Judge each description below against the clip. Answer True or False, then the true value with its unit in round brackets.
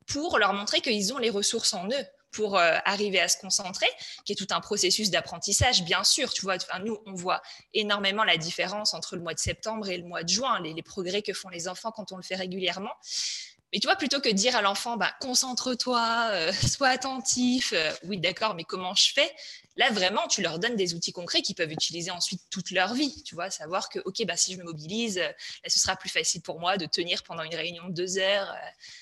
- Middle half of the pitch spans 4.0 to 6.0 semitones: True (4.4 semitones)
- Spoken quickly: True (240 wpm)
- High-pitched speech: True (195 Hz)